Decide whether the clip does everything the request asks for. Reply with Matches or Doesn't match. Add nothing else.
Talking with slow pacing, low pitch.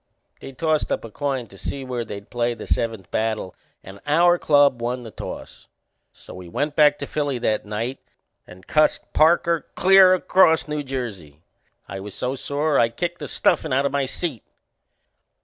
Doesn't match